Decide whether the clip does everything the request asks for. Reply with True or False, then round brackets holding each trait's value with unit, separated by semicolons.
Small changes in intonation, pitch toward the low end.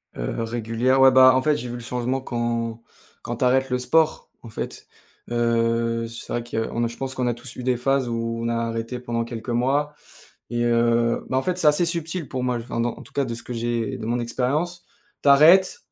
True (2.2 semitones; 120 Hz)